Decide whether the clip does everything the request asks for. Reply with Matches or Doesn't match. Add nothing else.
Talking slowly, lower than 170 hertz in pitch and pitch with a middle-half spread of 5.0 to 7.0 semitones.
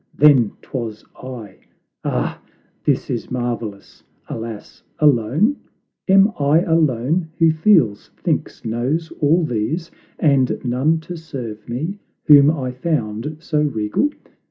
Matches